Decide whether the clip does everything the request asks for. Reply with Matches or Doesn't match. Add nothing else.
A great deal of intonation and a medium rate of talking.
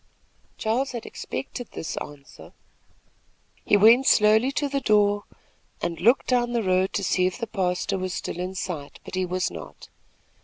Doesn't match